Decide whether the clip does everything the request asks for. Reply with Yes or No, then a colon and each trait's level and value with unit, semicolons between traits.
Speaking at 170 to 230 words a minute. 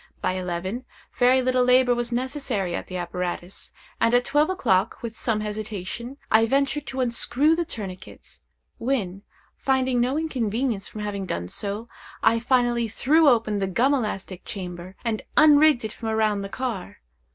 No: average, 160 wpm